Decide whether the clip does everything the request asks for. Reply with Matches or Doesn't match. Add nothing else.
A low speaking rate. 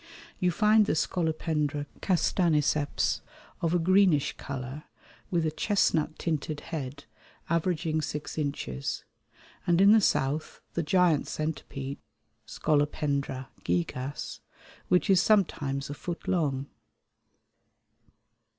Matches